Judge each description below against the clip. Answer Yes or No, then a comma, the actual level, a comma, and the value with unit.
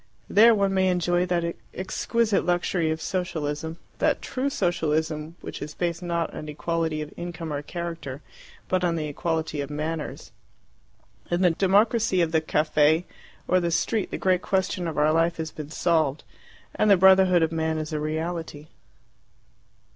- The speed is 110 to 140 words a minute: No, average, 160 wpm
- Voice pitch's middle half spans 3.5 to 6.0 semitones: No, narrow, 2.6 semitones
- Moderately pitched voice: Yes, medium, 165 Hz